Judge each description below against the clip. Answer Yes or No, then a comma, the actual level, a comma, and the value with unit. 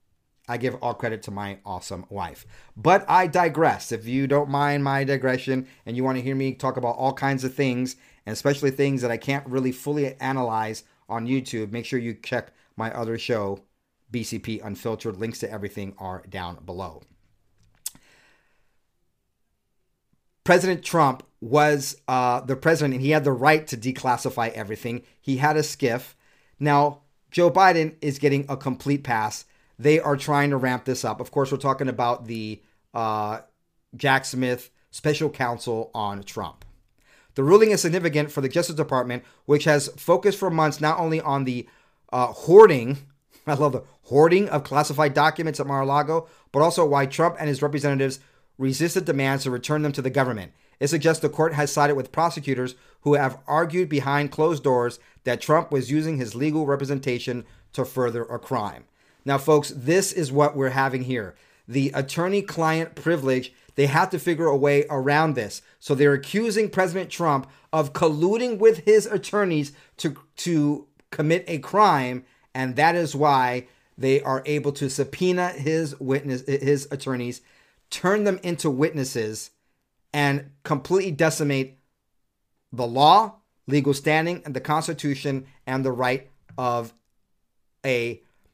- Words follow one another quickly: No, average, 160 wpm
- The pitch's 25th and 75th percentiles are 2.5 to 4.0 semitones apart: Yes, average, 3.6 semitones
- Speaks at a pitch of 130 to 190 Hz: Yes, medium, 140 Hz